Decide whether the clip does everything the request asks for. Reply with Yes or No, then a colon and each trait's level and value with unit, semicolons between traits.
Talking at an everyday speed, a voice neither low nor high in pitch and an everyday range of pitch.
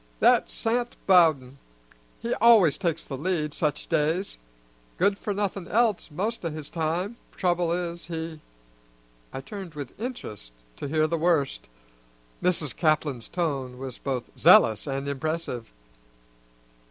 No: slow, 130 wpm; medium, 165 Hz; average, 4.4 semitones